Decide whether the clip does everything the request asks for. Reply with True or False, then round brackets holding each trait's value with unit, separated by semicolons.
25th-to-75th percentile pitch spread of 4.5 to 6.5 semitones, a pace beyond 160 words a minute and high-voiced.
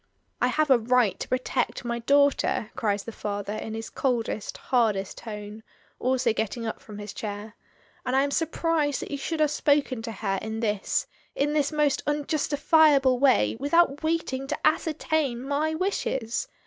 True (4.9 semitones; 170 wpm; 260 Hz)